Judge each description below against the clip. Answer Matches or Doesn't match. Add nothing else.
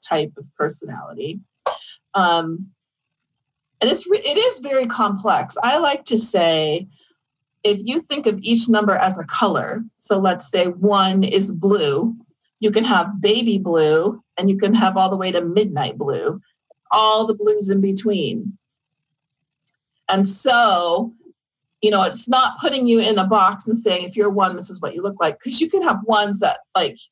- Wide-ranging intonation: Doesn't match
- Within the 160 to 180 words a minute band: Matches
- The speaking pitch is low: Doesn't match